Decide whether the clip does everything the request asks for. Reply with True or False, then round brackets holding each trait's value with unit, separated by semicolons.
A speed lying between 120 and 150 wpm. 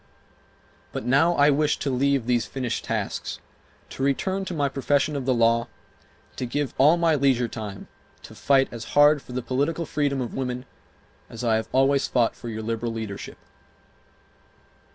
False (175 wpm)